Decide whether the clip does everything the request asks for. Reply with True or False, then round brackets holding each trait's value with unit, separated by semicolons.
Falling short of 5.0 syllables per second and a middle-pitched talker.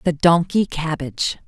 True (4.7 syllables/s; 160 Hz)